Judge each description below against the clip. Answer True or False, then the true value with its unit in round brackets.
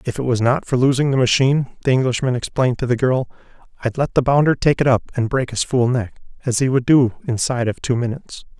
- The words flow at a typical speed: False (235 wpm)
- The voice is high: False (125 Hz)